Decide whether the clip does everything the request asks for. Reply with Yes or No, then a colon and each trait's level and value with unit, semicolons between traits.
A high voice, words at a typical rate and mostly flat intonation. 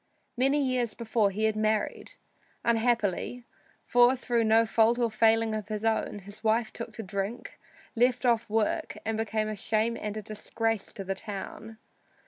Yes: high, 225 Hz; average, 165 wpm; narrow, 1.6 semitones